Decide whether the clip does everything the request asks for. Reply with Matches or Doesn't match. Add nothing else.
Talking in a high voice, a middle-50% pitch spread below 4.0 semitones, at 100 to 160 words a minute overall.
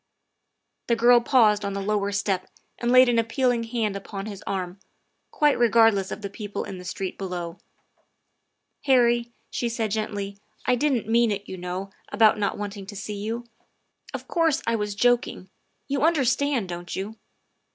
Doesn't match